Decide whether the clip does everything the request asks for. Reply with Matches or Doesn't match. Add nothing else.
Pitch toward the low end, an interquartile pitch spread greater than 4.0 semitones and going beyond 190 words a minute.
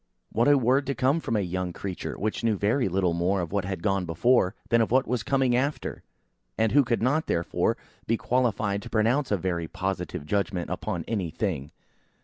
Matches